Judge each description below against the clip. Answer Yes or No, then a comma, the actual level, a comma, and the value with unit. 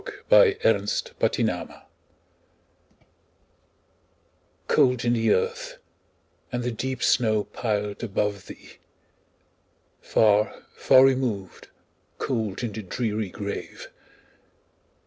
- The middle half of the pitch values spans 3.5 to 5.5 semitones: Yes, average, 3.9 semitones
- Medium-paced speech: No, slow, 90 wpm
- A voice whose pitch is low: Yes, low, 115 Hz